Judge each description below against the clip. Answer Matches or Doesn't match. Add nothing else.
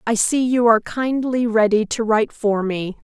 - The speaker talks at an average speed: Matches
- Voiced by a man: Doesn't match